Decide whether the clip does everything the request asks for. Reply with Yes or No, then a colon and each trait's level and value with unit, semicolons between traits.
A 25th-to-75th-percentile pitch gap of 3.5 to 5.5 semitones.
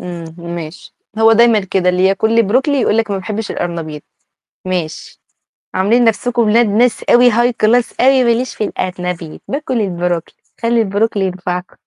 Yes: average, 4.7 semitones